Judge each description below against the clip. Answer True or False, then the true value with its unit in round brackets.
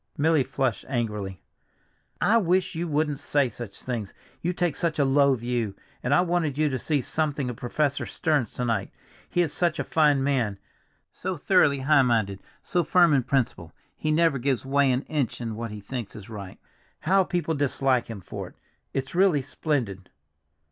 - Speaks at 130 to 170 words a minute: False (180 wpm)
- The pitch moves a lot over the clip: False (4.8 semitones)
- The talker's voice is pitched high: False (135 Hz)